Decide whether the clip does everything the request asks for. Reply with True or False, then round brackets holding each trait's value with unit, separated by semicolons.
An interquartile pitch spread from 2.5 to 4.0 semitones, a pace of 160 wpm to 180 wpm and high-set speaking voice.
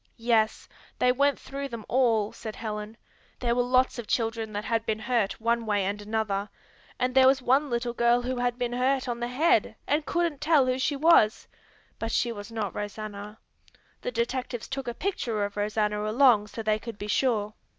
False (3.0 semitones; 195 wpm; 235 Hz)